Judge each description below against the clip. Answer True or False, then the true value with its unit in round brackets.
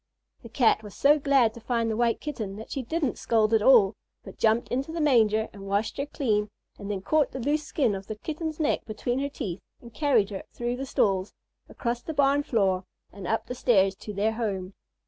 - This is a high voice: True (230 Hz)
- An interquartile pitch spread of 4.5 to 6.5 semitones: True (4.8 semitones)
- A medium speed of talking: False (220 wpm)